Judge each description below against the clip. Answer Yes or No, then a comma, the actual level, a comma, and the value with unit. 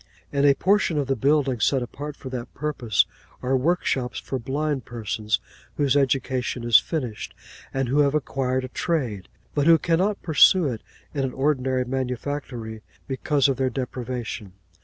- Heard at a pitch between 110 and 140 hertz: Yes, low, 135 Hz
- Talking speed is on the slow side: No, average, 160 wpm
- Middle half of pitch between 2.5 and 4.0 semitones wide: Yes, average, 2.8 semitones